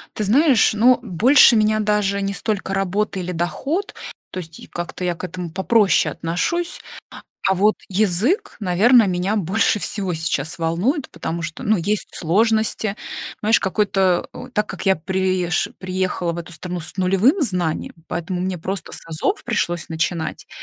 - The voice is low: No, high, 190 Hz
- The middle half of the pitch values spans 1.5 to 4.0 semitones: Yes, average, 3.5 semitones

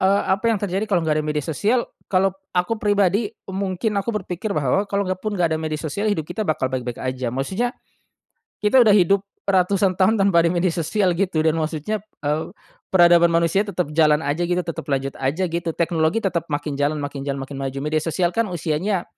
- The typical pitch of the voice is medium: Yes, medium, 175 Hz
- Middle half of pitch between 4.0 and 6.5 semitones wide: Yes, average, 4.4 semitones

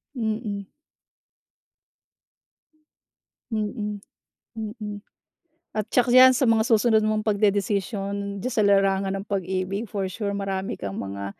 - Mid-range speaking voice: No, high, 205 Hz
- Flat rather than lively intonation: Yes, narrow, 2.0 semitones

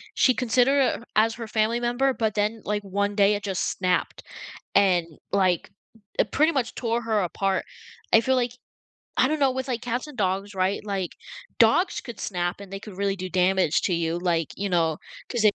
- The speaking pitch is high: Yes, high, 205 Hz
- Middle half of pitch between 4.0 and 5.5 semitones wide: Yes, average, 4.3 semitones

